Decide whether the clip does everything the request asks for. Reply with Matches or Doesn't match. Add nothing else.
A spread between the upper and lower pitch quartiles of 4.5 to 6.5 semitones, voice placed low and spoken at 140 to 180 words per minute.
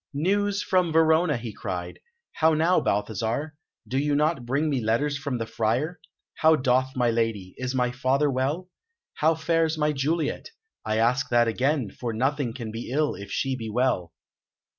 Matches